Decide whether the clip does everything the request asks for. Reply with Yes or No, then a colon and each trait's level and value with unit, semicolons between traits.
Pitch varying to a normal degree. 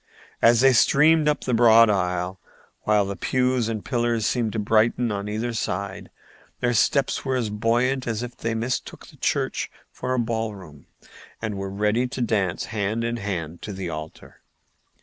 Yes: average, 3.3 semitones